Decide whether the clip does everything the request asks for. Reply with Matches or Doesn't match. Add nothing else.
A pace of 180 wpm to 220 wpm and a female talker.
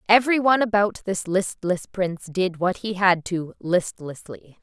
Doesn't match